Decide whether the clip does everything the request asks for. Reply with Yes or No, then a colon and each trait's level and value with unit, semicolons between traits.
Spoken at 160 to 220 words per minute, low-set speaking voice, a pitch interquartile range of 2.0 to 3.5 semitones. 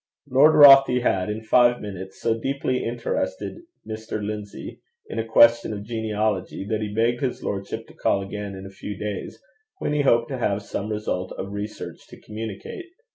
Yes: average, 180 wpm; low, 110 Hz; average, 2.9 semitones